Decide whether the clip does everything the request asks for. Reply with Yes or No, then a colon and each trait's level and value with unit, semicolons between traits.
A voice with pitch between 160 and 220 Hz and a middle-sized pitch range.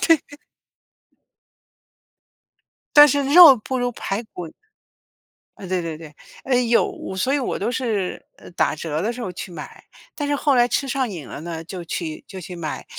No: high, 215 Hz; wide, 7.7 semitones